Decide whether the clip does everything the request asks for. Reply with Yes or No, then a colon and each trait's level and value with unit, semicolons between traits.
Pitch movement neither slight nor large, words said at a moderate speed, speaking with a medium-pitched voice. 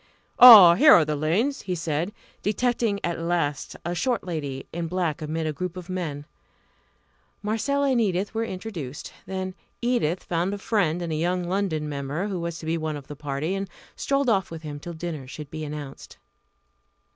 Yes: average, 4.4 semitones; average, 185 wpm; medium, 175 Hz